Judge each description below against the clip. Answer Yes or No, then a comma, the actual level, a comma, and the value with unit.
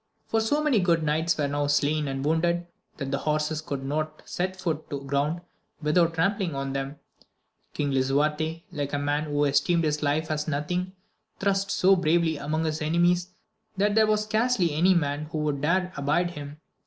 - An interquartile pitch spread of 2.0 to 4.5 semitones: Yes, average, 3.4 semitones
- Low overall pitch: No, medium, 155 Hz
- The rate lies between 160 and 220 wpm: Yes, average, 180 wpm